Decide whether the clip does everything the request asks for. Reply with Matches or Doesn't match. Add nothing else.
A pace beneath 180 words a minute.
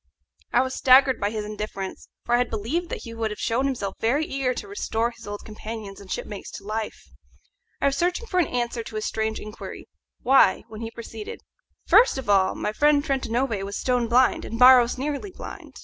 Doesn't match